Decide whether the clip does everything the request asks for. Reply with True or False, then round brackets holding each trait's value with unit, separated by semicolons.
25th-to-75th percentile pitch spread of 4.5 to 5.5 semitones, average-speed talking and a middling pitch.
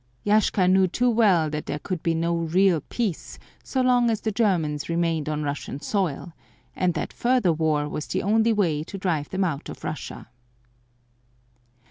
True (5.0 semitones; 170 wpm; 180 Hz)